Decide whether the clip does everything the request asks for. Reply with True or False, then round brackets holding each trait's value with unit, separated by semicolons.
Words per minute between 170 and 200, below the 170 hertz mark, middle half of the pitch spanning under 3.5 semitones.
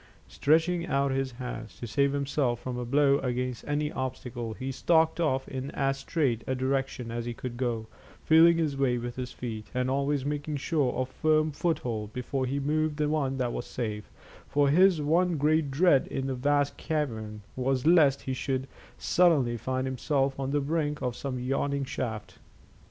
True (180 wpm; 135 Hz; 2.8 semitones)